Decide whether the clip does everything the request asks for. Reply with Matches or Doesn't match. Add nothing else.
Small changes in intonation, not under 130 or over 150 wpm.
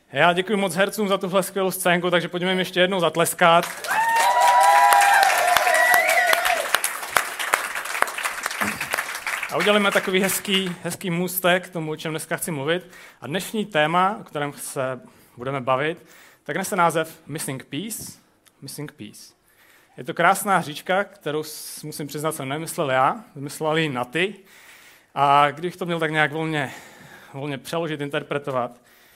Doesn't match